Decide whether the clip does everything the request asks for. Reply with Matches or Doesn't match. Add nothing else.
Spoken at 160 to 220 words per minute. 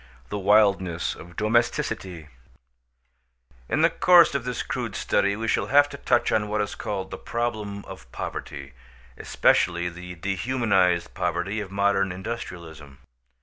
Doesn't match